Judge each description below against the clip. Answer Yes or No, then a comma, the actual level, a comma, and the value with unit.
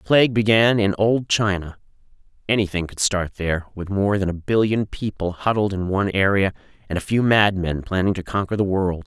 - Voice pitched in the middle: No, low, 100 Hz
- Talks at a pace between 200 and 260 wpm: No, average, 190 wpm